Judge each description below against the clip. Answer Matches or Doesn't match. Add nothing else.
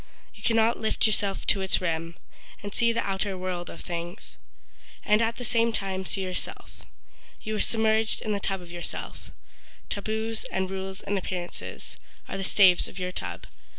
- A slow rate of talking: Doesn't match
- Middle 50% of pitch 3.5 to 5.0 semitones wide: Doesn't match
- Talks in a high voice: Matches